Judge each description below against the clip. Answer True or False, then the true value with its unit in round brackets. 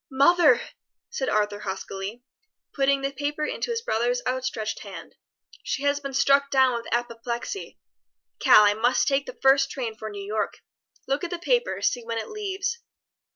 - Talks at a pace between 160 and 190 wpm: True (165 wpm)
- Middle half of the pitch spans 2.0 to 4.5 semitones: True (3.9 semitones)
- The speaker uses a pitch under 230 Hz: False (265 Hz)